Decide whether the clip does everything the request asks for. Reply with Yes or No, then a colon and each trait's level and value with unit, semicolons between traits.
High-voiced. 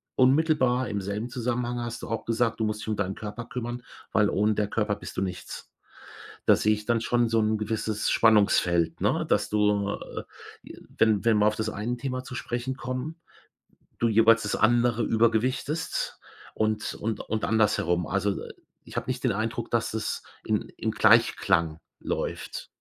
No: low, 110 Hz